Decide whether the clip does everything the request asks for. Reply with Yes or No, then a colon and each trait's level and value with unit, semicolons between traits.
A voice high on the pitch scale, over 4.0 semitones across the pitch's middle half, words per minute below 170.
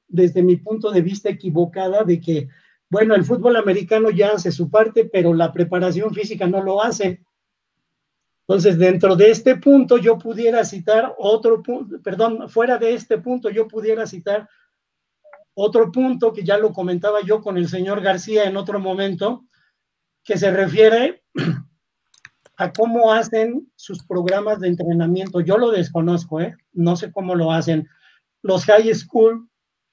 No: high, 205 Hz; average, 3.7 semitones; average, 155 wpm